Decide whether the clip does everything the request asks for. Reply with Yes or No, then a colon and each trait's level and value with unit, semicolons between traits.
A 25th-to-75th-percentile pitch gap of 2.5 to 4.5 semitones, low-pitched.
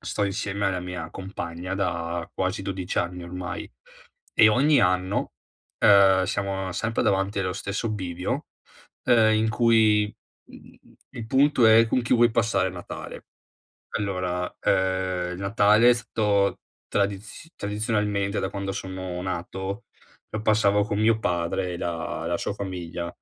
Yes: average, 2.8 semitones; low, 100 Hz